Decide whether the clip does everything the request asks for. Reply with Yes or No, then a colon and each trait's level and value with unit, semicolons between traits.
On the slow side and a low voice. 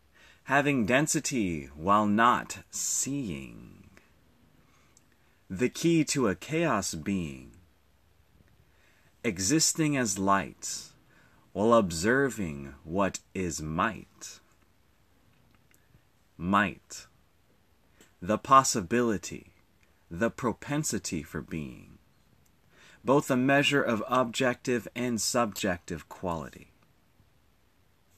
Yes: slow, 70 wpm; low, 105 Hz